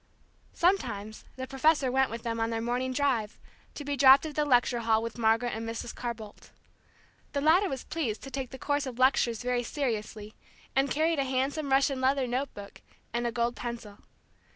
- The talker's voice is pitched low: No, very high, 255 Hz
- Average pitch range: Yes, average, 3.2 semitones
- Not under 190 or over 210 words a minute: Yes, average, 195 wpm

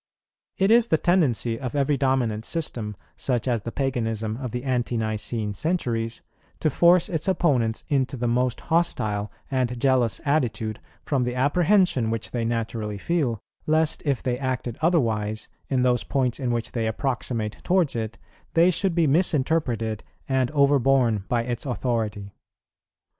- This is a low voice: Yes, low, 125 Hz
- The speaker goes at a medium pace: Yes, average, 150 wpm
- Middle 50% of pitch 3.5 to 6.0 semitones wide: Yes, average, 4.2 semitones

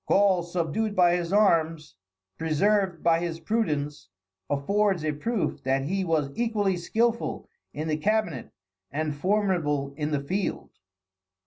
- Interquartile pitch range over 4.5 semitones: Yes, average, 5.1 semitones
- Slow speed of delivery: Yes, slow, 130 wpm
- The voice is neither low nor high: Yes, medium, 170 Hz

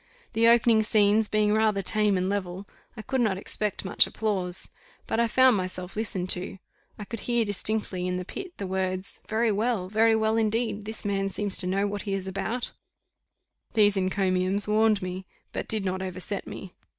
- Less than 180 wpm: No, average, 185 wpm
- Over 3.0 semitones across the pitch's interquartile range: No, average, 2.7 semitones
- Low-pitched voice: No, high, 205 Hz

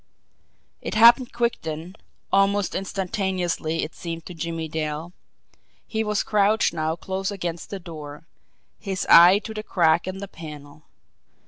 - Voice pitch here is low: No, medium, 180 Hz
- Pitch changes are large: No, average, 3.7 semitones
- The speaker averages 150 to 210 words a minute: No, average, 140 wpm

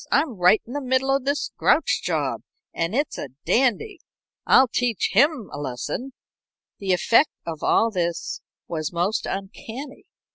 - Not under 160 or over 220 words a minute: No, average, 150 wpm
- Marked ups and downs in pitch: Yes, wide, 7.3 semitones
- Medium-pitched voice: No, high, 230 Hz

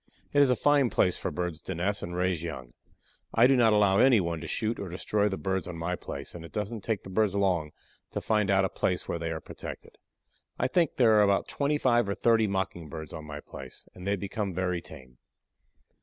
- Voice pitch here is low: Yes, very low, 95 Hz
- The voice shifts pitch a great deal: No, average, 4.2 semitones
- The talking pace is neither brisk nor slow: No, fast, 230 wpm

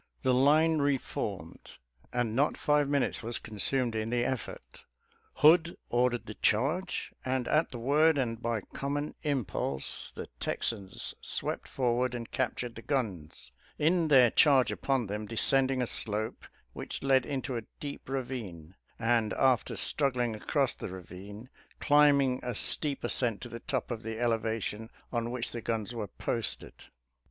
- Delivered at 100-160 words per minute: Yes, average, 155 wpm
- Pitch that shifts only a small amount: No, average, 3.6 semitones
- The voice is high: No, low, 125 Hz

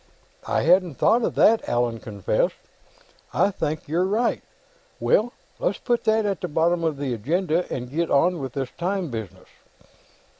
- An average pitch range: No, wide, 6.3 semitones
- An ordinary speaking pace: Yes, average, 160 wpm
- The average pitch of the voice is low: No, medium, 170 Hz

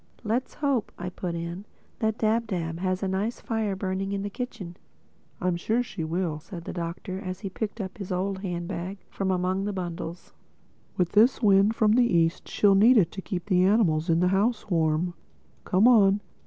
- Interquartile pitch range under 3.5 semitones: Yes, average, 3.1 semitones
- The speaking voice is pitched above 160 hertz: Yes, high, 190 Hz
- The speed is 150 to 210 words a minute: Yes, average, 190 wpm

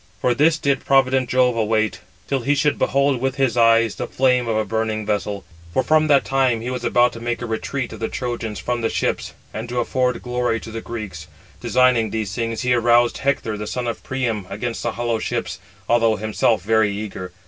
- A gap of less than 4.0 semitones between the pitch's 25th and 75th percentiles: Yes, narrow, 2.4 semitones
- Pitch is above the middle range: No, low, 120 Hz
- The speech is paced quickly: Yes, fast, 210 wpm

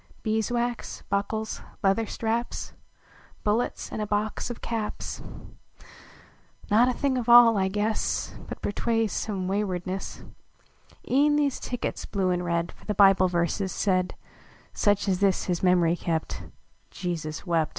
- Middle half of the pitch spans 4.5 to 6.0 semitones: No, average, 3.7 semitones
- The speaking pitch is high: Yes, high, 205 Hz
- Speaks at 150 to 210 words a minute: No, average, 140 wpm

